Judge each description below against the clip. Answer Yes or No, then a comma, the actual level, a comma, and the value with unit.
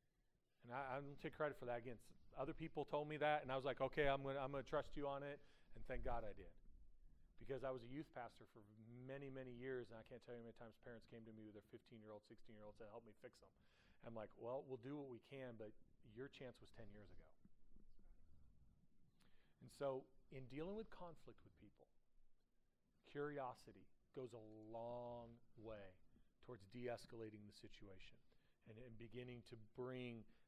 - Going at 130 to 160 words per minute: No, fast, 205 wpm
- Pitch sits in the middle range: No, low, 120 Hz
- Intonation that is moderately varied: Yes, average, 3.6 semitones